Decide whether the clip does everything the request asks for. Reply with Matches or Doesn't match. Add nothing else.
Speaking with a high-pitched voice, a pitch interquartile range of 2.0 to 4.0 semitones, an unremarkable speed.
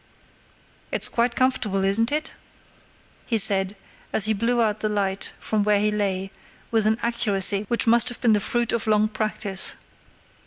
Matches